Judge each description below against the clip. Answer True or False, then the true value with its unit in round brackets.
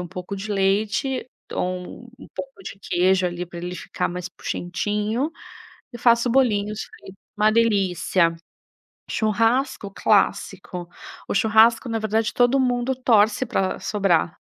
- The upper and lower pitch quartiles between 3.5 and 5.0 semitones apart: True (4.2 semitones)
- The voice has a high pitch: True (210 Hz)